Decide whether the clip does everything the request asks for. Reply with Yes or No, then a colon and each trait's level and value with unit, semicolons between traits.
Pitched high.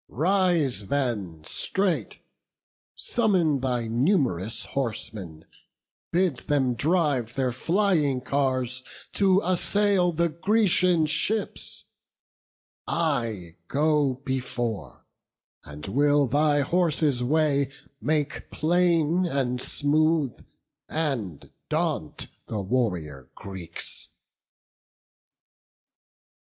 No: medium, 140 Hz